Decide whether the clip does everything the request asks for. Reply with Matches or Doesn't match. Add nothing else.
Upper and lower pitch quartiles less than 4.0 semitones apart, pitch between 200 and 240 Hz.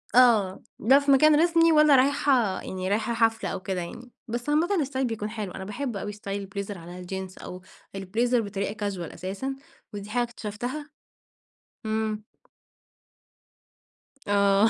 Doesn't match